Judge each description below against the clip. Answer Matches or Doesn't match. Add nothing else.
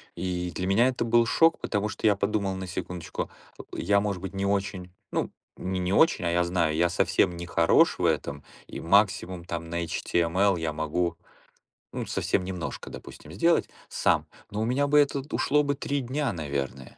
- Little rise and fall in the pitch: Doesn't match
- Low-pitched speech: Matches